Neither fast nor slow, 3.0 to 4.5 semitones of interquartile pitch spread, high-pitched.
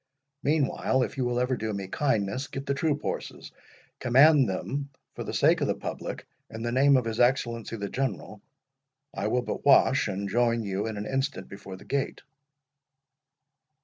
No: average, 175 wpm; average, 3.9 semitones; low, 125 Hz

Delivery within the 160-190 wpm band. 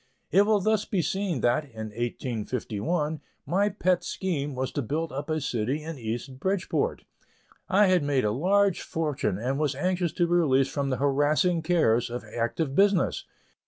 Yes: average, 170 wpm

